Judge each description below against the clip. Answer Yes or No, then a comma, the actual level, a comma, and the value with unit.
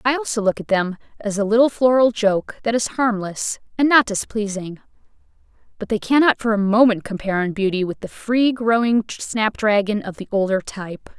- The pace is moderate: Yes, average, 180 wpm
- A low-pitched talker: No, high, 215 Hz